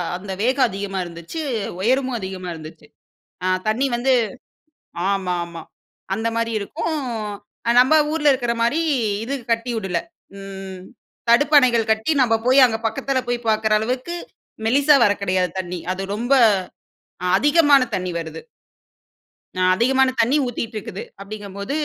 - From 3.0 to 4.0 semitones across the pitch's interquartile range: No, average, 5.1 semitones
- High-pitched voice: Yes, high, 225 Hz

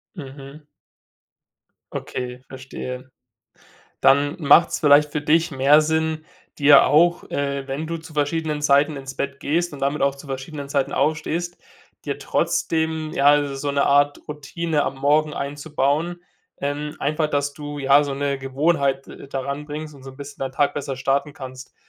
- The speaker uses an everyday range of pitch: No, narrow, 1.8 semitones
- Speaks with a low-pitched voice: No, medium, 145 Hz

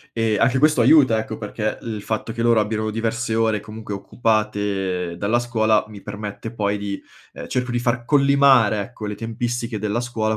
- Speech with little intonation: Yes, narrow, 2.2 semitones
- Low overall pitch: Yes, low, 110 Hz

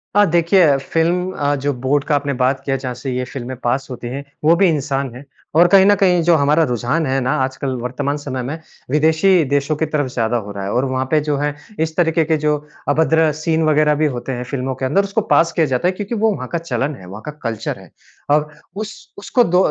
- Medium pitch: Yes, medium, 145 Hz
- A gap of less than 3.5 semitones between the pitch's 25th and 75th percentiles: No, average, 3.9 semitones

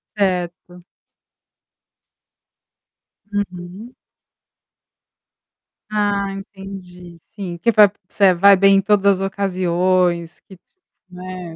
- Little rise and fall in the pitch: Yes, narrow, 2.0 semitones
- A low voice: No, medium, 185 Hz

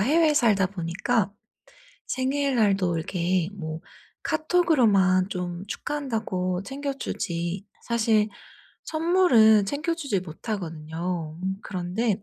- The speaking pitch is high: Yes, high, 200 Hz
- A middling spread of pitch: No, wide, 6.6 semitones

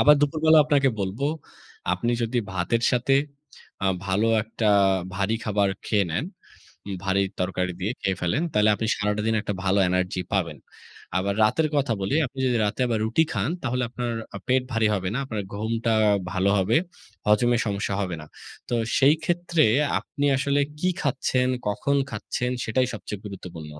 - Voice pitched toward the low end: Yes, low, 110 Hz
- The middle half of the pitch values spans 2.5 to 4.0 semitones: No, average, 4.9 semitones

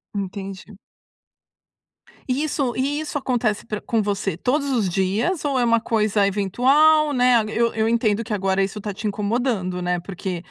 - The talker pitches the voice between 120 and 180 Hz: No, high, 220 Hz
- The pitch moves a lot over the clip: No, average, 4.3 semitones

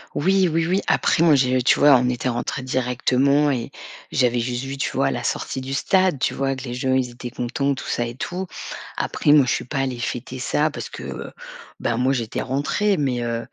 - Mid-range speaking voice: No, low, 130 Hz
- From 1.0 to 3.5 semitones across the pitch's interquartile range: Yes, average, 2.8 semitones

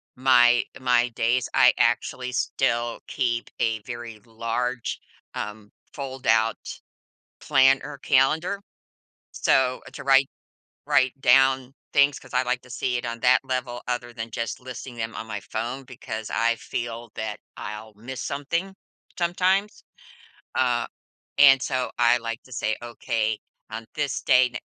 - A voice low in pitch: Yes, low, 125 Hz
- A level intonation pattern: Yes, narrow, 2.3 semitones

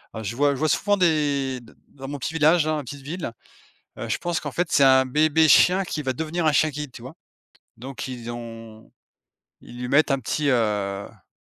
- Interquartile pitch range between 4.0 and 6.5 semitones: Yes, average, 4.4 semitones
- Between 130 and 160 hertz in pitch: Yes, medium, 140 Hz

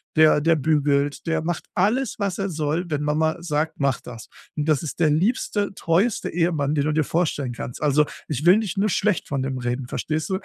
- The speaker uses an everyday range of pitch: Yes, average, 3.5 semitones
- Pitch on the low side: No, medium, 155 Hz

